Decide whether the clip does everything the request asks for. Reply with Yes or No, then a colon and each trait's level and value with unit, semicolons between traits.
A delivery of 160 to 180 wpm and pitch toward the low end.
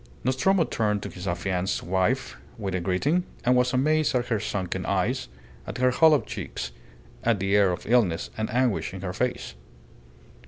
Yes: average, 170 wpm; low, 110 Hz